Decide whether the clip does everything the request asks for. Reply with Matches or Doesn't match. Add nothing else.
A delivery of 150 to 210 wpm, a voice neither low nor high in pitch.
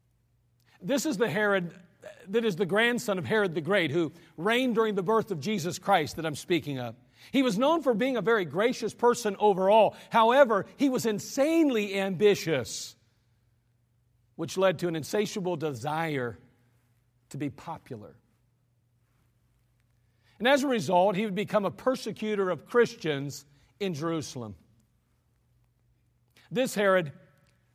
Doesn't match